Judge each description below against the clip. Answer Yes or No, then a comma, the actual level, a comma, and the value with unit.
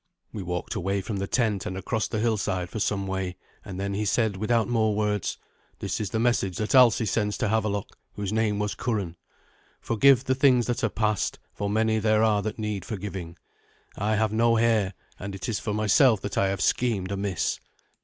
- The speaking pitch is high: No, low, 105 Hz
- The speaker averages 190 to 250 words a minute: Yes, average, 200 wpm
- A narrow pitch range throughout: Yes, narrow, 2.3 semitones